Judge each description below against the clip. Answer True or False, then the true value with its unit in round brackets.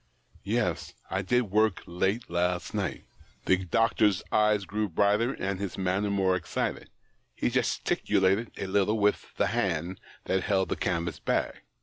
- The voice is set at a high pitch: False (95 Hz)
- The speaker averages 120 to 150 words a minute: True (145 wpm)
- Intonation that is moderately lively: False (2.3 semitones)